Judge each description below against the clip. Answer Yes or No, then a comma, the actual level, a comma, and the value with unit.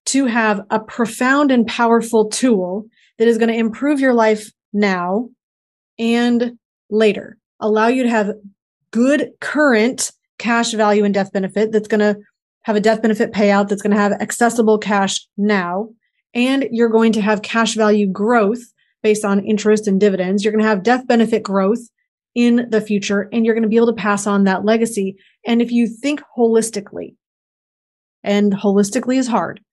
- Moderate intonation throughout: No, narrow, 2.3 semitones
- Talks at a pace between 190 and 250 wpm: No, average, 175 wpm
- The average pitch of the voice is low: No, high, 220 Hz